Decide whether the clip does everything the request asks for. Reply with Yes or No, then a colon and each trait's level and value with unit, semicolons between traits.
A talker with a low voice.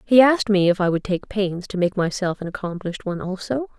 No: high, 195 Hz